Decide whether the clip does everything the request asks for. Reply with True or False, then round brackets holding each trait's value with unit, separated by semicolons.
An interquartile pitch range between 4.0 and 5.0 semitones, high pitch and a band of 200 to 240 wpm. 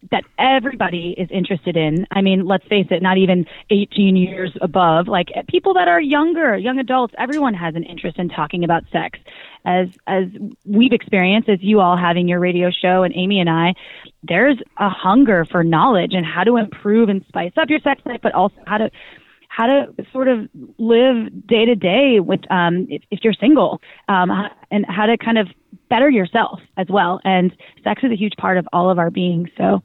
True (4.4 semitones; 195 Hz; 205 wpm)